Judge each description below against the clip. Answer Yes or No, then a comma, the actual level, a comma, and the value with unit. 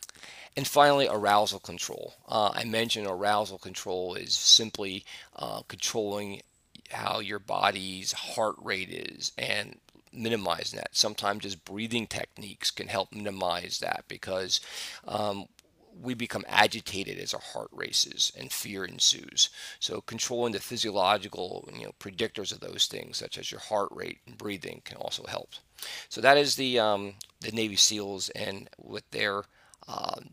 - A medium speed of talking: Yes, average, 145 wpm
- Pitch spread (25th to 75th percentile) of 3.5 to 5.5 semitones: No, narrow, 2.6 semitones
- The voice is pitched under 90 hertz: No, low, 105 Hz